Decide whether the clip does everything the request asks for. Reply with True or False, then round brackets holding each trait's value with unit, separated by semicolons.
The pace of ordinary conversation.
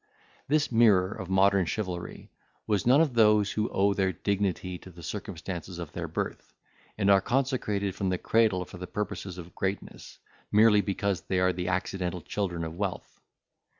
True (170 wpm)